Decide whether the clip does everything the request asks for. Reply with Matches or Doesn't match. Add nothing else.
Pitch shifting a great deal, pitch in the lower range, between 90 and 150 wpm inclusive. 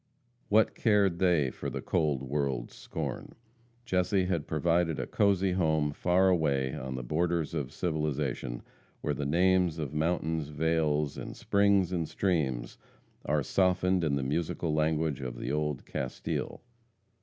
Doesn't match